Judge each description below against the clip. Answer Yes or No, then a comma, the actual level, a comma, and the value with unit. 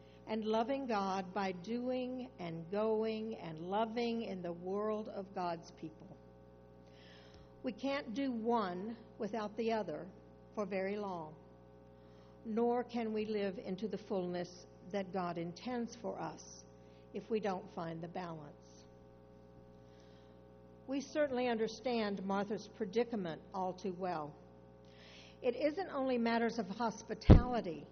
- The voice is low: No, high, 195 Hz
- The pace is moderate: No, slow, 125 wpm